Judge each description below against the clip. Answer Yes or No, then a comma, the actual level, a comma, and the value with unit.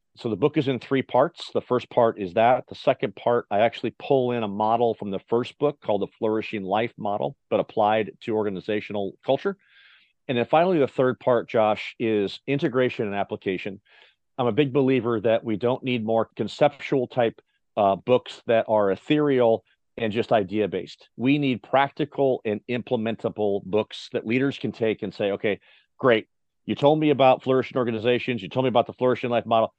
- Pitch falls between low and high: No, low, 120 Hz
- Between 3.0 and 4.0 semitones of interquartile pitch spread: Yes, average, 3.5 semitones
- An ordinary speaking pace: Yes, average, 190 wpm